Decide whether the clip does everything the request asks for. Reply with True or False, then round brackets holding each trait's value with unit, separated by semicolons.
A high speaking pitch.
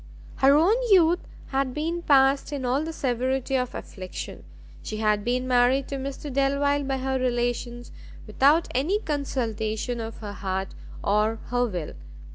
True (260 Hz)